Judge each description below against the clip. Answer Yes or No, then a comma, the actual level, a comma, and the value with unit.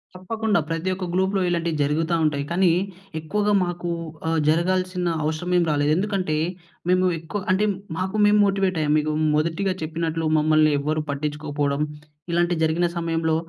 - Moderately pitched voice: Yes, medium, 170 Hz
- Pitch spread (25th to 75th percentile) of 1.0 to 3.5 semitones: Yes, average, 3.1 semitones